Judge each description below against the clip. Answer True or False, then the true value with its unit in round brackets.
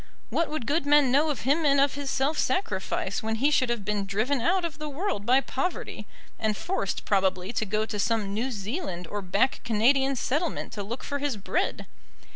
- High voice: True (260 Hz)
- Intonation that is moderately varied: False (5.7 semitones)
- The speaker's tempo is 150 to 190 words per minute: False (205 wpm)